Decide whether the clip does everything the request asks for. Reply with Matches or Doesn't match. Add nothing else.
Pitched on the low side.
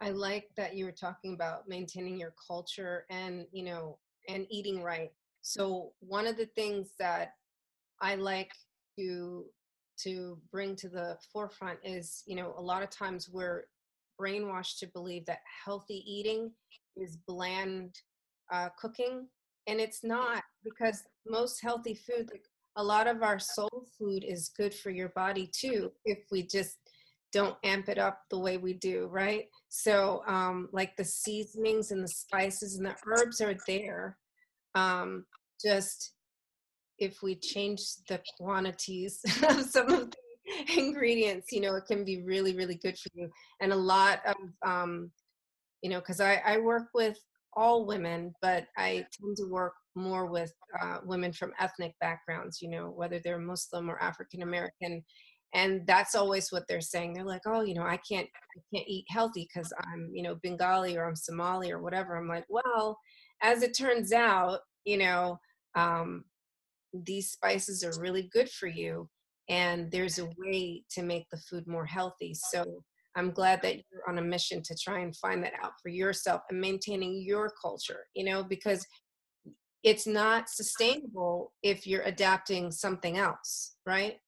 Doesn't match